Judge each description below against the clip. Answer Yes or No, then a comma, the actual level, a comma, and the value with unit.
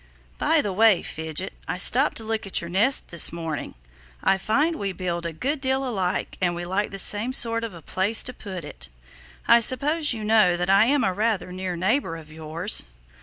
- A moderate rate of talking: No, fast, 210 wpm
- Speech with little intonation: No, average, 4.8 semitones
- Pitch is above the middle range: Yes, high, 195 Hz